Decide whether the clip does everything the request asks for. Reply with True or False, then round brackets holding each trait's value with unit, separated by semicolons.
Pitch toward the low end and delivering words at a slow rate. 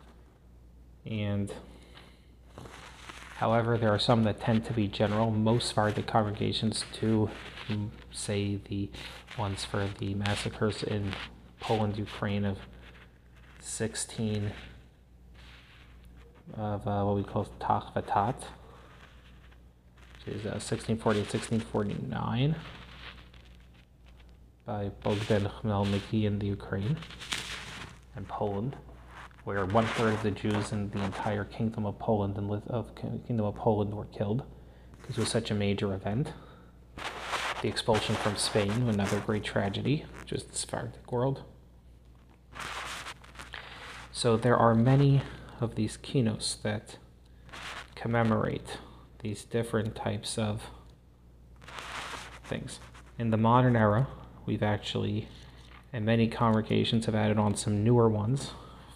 True (105 Hz; 115 wpm)